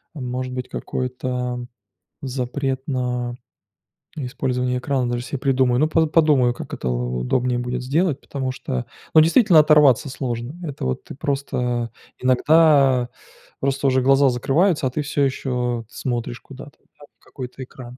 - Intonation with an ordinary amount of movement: No, narrow, 2.3 semitones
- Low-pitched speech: Yes, low, 130 Hz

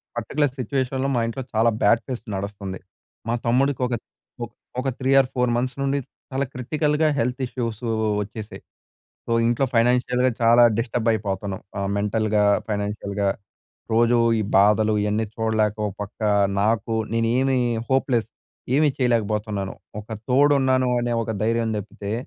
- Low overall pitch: Yes, low, 115 Hz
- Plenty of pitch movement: No, average, 3.4 semitones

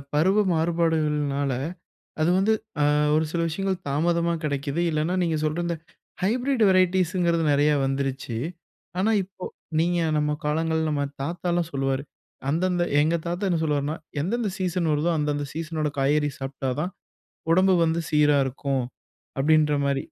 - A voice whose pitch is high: No, medium, 160 Hz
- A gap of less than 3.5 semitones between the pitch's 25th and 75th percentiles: Yes, average, 3.1 semitones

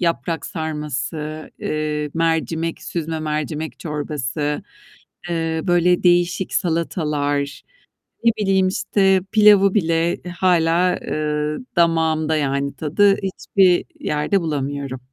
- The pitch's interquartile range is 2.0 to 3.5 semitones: Yes, average, 2.8 semitones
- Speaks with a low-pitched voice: No, medium, 160 Hz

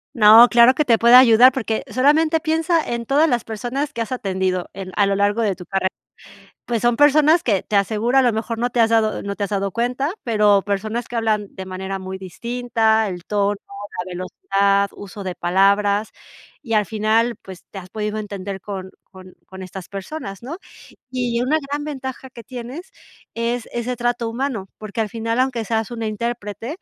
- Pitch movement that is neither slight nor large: Yes, average, 3.5 semitones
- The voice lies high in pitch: Yes, high, 225 Hz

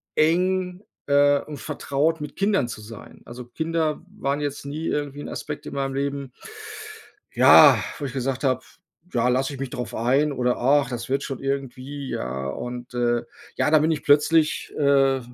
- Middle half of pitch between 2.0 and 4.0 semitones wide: Yes, average, 2.9 semitones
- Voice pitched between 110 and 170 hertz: Yes, medium, 140 Hz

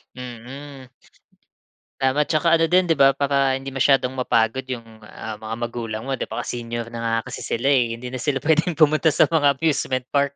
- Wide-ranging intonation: No, average, 3.3 semitones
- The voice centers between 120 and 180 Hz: Yes, low, 135 Hz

